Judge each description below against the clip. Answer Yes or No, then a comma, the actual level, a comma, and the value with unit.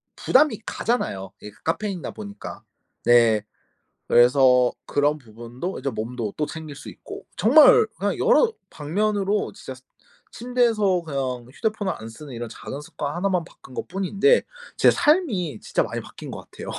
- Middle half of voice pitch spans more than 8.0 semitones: Yes, wide, 8.9 semitones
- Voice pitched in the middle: Yes, medium, 160 Hz